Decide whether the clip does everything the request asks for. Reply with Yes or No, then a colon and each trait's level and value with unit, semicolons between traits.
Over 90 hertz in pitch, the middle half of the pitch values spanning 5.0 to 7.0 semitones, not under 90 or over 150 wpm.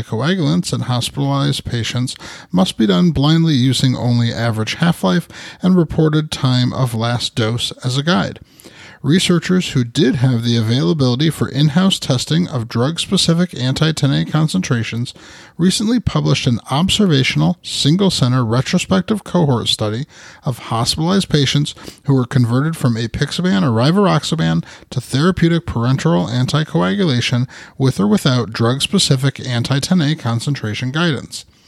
Yes: medium, 140 Hz; wide, 5.5 semitones; slow, 135 wpm